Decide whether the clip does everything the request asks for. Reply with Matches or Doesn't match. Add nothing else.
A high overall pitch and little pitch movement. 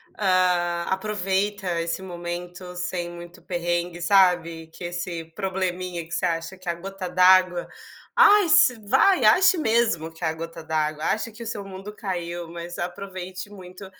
Doesn't match